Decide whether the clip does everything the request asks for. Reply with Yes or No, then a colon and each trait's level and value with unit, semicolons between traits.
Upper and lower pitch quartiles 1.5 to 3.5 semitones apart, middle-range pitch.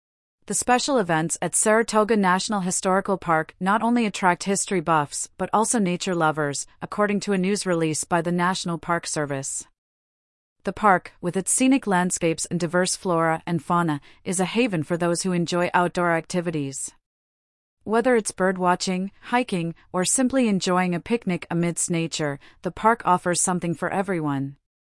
Yes: average, 3.1 semitones; medium, 180 Hz